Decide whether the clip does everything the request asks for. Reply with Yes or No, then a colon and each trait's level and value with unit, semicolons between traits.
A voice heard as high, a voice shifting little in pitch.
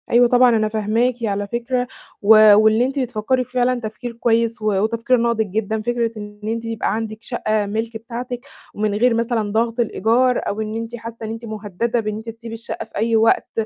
Yes: high, 225 Hz; narrow, 1.7 semitones